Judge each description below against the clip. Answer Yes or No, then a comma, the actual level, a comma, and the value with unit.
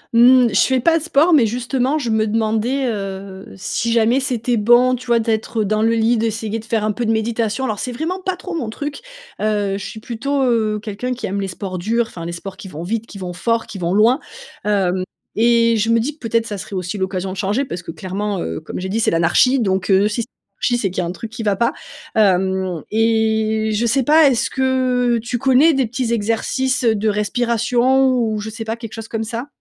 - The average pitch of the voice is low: No, high, 225 Hz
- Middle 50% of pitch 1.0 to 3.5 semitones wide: Yes, average, 3.2 semitones